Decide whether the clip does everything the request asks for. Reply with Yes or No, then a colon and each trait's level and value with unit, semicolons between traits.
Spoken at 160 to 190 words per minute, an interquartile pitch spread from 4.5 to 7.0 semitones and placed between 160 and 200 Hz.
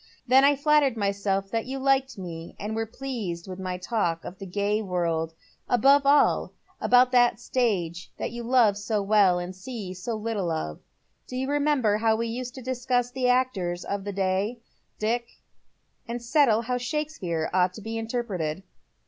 No: average, 175 wpm; average, 5.0 semitones; high, 220 Hz